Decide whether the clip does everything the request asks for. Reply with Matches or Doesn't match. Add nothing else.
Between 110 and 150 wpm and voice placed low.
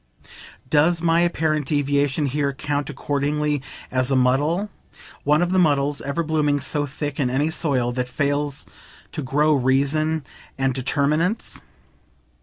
Doesn't match